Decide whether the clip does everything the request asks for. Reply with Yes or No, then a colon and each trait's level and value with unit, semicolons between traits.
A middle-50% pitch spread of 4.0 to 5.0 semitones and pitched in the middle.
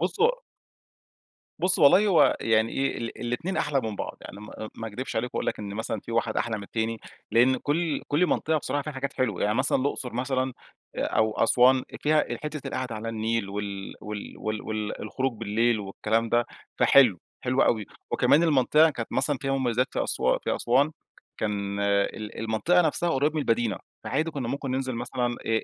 No: average, 4.3 semitones; low, 120 Hz